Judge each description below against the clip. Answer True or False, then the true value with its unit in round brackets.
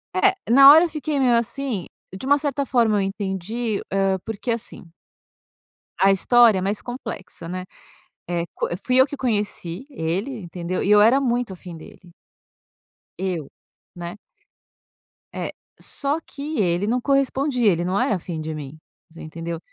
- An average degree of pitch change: False (6.2 semitones)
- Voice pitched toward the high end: True (205 Hz)